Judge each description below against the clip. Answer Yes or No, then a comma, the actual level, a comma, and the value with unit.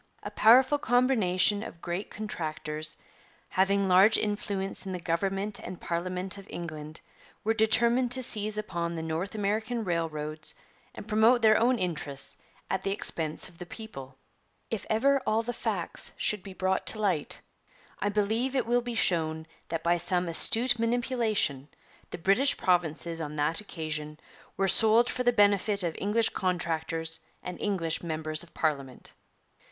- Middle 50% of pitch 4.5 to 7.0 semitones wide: Yes, average, 4.9 semitones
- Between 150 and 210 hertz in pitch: Yes, high, 190 Hz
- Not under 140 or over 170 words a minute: Yes, average, 155 wpm